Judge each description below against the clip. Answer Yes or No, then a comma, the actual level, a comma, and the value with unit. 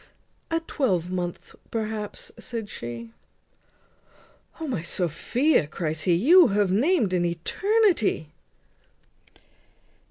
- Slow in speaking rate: Yes, slow, 90 wpm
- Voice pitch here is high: Yes, high, 200 Hz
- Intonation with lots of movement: Yes, wide, 8.2 semitones